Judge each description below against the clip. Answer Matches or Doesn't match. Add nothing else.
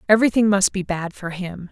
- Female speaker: Matches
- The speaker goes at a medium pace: Doesn't match